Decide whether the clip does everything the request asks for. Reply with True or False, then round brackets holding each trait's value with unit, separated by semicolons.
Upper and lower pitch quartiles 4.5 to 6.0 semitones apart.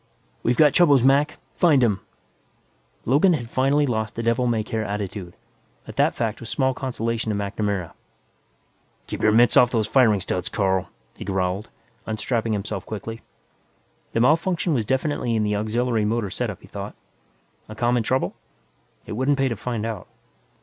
False (3.7 semitones)